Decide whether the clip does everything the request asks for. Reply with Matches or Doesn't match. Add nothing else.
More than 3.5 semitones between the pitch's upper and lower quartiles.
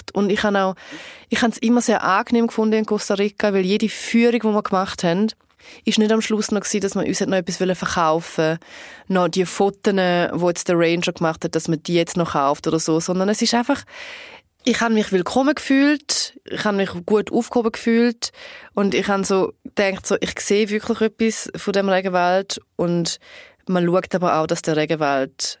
Matches